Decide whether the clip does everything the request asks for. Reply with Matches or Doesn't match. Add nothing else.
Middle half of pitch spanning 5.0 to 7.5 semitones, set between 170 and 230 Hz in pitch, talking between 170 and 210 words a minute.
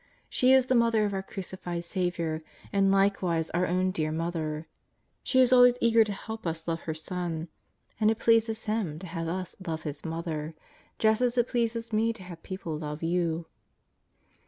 Matches